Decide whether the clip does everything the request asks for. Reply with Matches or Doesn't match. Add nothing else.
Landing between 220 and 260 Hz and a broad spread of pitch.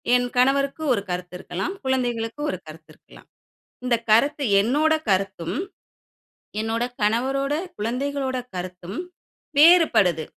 Matches